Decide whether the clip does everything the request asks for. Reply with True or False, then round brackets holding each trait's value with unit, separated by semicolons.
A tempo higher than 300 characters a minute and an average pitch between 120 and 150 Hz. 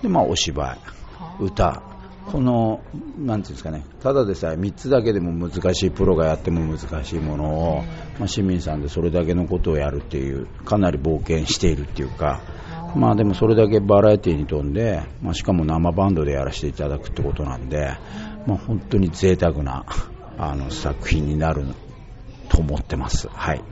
False (335 characters per minute; 85 Hz)